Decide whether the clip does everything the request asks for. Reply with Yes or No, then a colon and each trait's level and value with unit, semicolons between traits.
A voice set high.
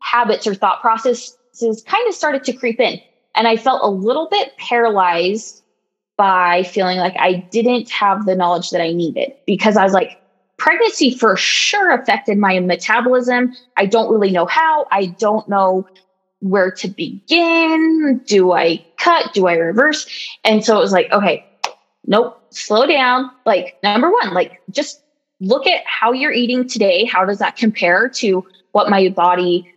Yes: high, 220 Hz